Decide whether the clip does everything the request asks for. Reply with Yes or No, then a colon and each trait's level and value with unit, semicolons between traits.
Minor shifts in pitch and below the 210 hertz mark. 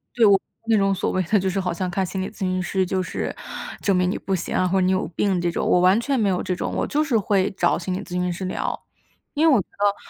Yes: narrow, 1.7 semitones; high, 190 Hz